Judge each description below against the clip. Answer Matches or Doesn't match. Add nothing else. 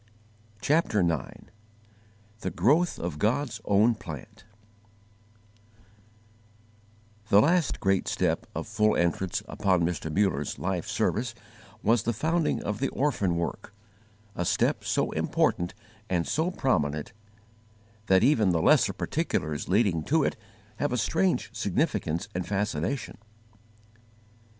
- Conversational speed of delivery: Doesn't match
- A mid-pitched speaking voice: Doesn't match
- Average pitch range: Doesn't match